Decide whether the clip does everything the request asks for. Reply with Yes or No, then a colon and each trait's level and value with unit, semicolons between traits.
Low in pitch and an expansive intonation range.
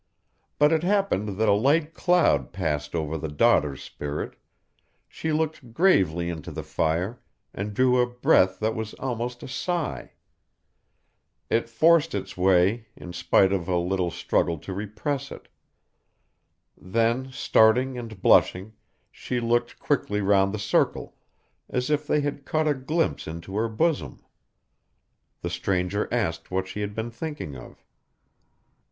Yes: low, 110 Hz; wide, 6.3 semitones